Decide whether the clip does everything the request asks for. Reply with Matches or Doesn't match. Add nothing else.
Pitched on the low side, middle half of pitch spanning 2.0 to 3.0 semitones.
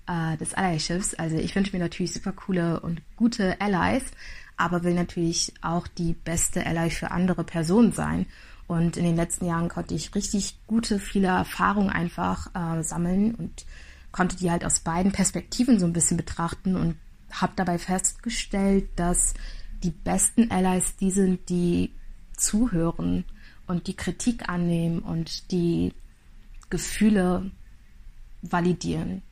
Doesn't match